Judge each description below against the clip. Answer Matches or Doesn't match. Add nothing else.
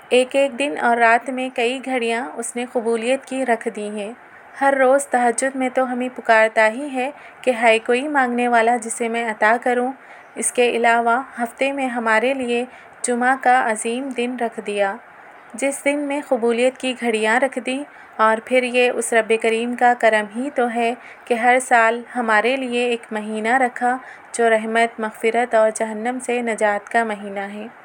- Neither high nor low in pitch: Doesn't match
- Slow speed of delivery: Doesn't match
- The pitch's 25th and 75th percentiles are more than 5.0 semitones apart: Doesn't match